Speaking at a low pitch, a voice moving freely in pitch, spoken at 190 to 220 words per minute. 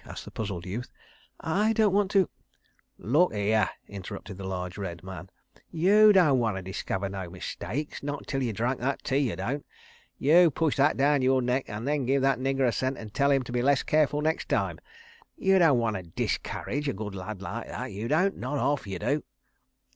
Yes: low, 130 Hz; wide, 6.5 semitones; average, 200 wpm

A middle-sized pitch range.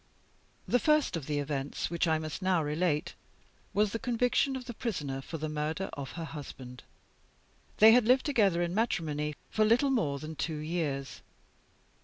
No: wide, 6.9 semitones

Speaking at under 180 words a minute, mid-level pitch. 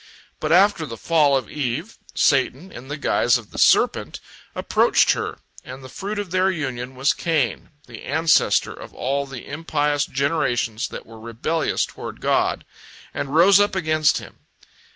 Yes: average, 160 wpm; medium, 145 Hz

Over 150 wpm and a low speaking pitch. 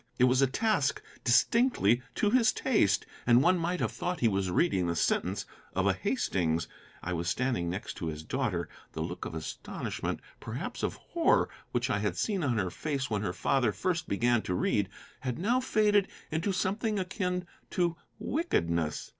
Yes: average, 180 wpm; low, 130 Hz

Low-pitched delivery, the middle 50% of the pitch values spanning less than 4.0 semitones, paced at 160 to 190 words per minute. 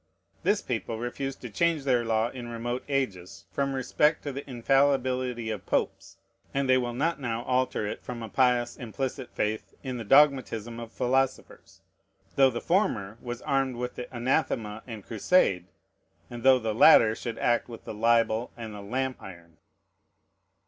Yes: low, 120 Hz; average, 2.8 semitones; average, 165 wpm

